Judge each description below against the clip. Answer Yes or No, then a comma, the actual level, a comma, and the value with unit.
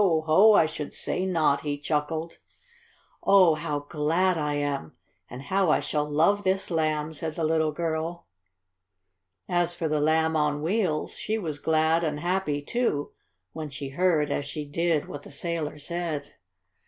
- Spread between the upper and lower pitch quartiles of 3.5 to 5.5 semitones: No, narrow, 2.5 semitones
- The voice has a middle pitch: Yes, medium, 160 Hz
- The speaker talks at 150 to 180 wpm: Yes, average, 160 wpm